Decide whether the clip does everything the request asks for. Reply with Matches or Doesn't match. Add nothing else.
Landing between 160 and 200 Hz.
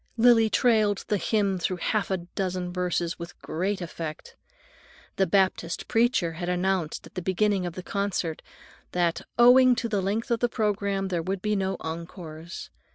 Matches